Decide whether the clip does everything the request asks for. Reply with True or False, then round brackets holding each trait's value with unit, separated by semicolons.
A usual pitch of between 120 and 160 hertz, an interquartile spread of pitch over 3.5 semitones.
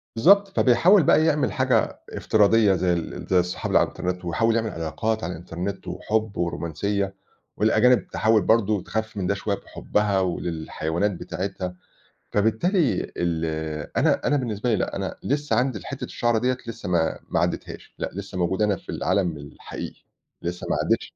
False (105 Hz; 4.1 semitones)